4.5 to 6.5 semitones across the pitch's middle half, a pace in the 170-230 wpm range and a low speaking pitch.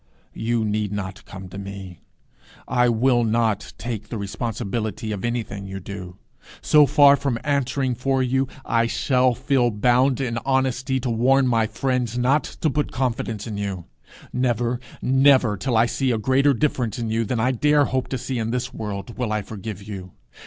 No: average, 3.5 semitones; average, 180 wpm; low, 120 Hz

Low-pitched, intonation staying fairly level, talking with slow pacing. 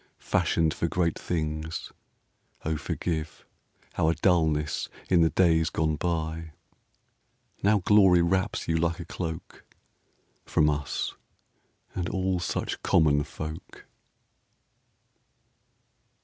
Yes: very low, 80 Hz; narrow, 2.0 semitones; slow, 100 wpm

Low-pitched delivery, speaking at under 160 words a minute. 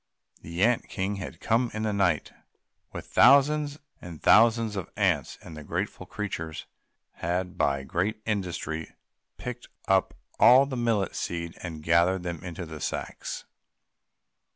Yes: very low, 95 Hz; average, 140 wpm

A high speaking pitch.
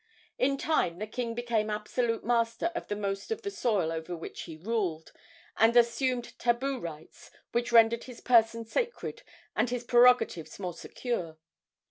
Yes: high, 230 Hz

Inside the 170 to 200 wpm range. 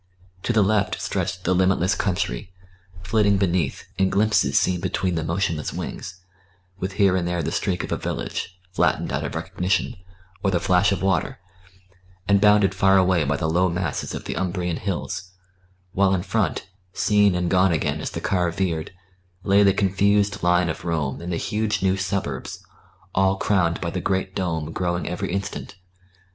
Yes: average, 175 wpm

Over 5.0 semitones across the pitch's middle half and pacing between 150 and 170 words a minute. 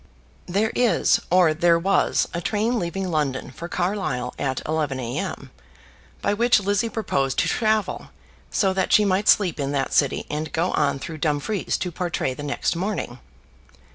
Yes: wide, 5.6 semitones; average, 165 wpm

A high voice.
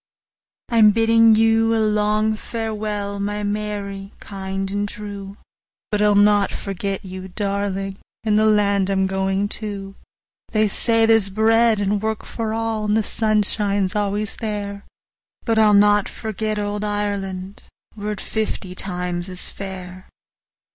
Yes: high, 205 Hz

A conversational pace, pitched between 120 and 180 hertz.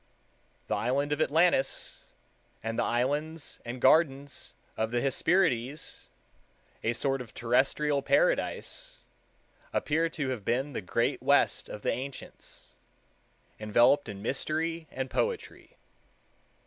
No: slow, 115 wpm; low, 135 Hz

